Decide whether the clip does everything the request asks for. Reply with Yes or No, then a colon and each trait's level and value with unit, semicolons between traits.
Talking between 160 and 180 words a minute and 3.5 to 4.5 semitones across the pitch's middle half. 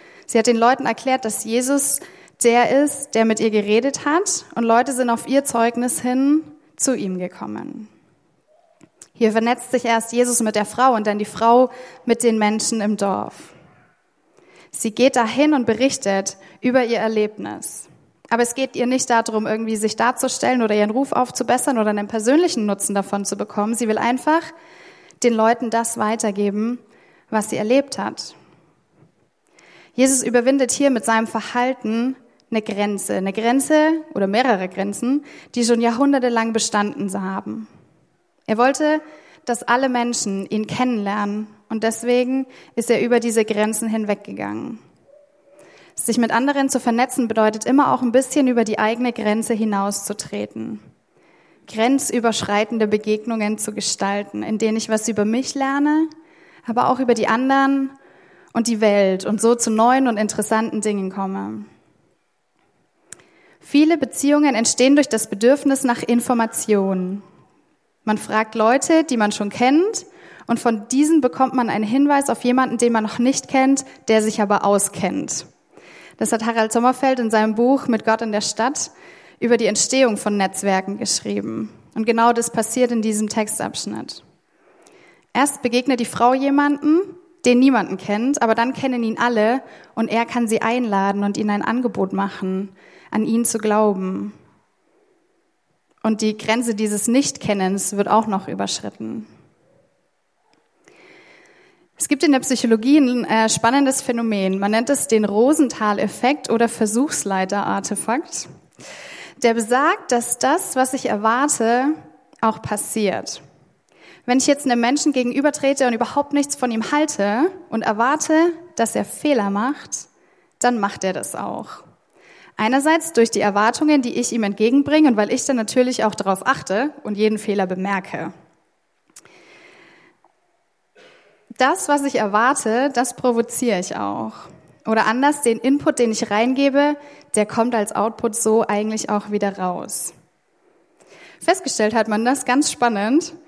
No: average, 145 wpm; average, 4.0 semitones